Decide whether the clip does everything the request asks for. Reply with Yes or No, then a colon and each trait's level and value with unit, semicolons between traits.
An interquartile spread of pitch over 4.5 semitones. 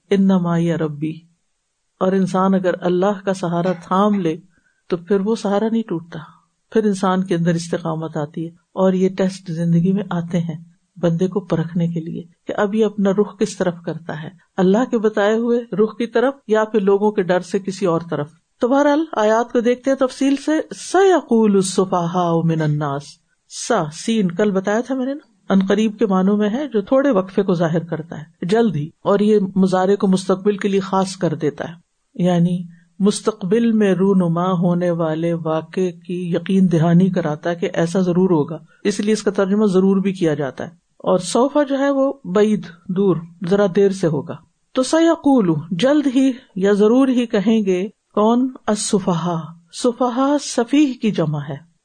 No: average, 4.0 semitones